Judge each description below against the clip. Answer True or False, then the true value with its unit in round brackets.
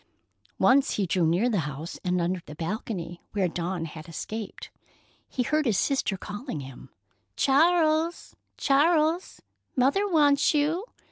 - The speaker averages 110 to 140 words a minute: True (135 wpm)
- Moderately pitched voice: False (220 Hz)